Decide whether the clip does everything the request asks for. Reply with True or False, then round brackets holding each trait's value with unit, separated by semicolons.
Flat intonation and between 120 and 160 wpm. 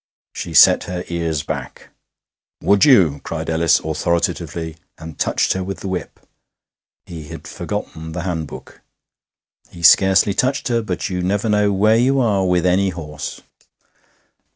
False (3.6 semitones; 145 wpm)